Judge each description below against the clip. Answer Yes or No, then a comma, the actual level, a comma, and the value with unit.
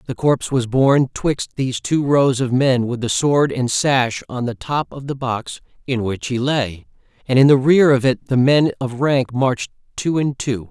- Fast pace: Yes, fast, 220 wpm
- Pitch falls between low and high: No, low, 130 Hz